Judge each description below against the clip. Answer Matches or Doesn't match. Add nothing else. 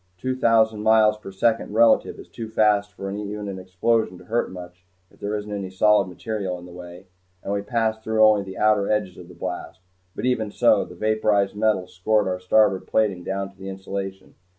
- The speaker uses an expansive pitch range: Doesn't match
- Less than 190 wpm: Doesn't match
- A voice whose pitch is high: Doesn't match